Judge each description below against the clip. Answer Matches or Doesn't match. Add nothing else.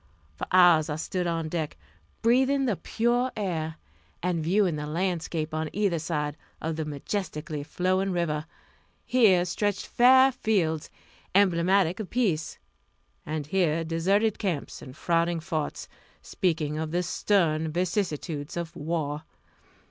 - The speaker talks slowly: Matches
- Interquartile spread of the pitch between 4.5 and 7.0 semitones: Doesn't match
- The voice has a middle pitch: Matches